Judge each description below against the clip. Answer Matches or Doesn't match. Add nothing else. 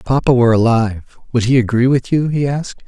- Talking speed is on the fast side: Matches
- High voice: Doesn't match